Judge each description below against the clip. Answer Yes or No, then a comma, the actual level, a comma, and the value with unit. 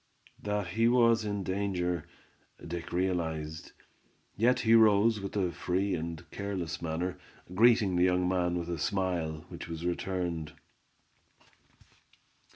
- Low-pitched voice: Yes, very low, 90 Hz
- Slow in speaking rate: Yes, slow, 125 wpm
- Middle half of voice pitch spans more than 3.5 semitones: No, average, 3.0 semitones